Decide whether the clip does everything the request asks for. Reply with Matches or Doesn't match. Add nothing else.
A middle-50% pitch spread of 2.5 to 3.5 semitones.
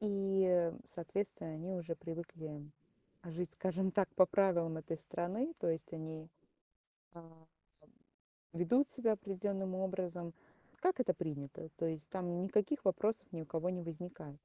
Matches